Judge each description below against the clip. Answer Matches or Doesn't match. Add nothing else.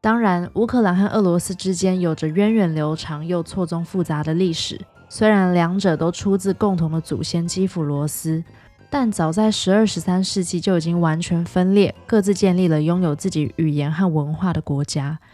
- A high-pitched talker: Doesn't match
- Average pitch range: Matches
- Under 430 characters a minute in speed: Matches